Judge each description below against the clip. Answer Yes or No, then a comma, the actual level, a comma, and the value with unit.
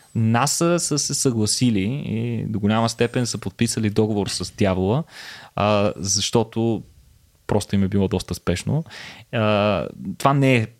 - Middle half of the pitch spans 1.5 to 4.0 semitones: Yes, average, 2.9 semitones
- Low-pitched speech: Yes, low, 110 Hz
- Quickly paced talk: No, average, 140 wpm